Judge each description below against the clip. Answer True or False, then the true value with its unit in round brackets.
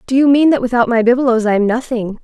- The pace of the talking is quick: True (240 wpm)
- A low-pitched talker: False (240 Hz)